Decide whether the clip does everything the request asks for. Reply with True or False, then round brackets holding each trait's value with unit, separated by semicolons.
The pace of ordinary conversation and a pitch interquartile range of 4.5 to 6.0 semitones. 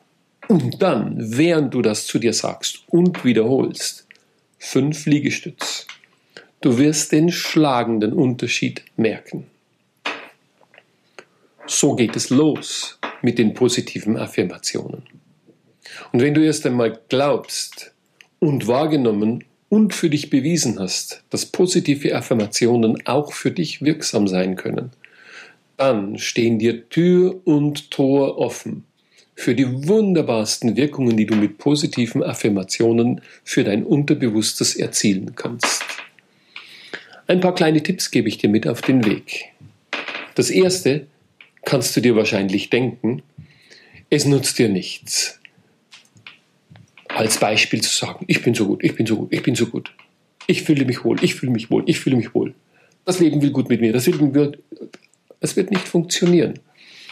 True (140 wpm; 5.6 semitones)